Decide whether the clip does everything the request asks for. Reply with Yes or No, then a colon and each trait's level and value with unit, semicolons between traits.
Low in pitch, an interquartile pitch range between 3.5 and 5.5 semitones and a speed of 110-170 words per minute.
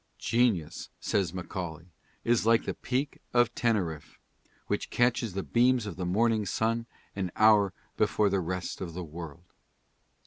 Yes: low, 100 Hz; average, 4.6 semitones; average, 145 wpm